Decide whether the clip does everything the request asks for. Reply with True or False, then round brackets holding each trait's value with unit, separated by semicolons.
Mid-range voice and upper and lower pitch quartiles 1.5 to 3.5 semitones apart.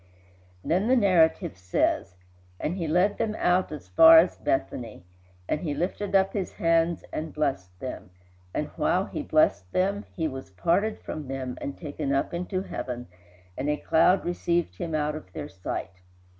False (160 Hz; 5.3 semitones)